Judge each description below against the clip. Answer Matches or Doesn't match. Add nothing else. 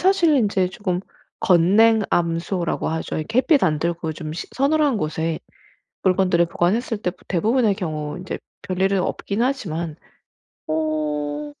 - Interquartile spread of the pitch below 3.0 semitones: Doesn't match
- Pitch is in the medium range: Matches